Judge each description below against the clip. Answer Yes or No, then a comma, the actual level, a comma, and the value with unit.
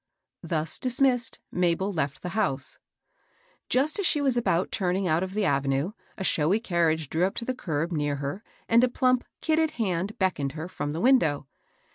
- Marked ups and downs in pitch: Yes, wide, 7.2 semitones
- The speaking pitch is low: No, medium, 185 Hz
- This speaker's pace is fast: No, average, 180 wpm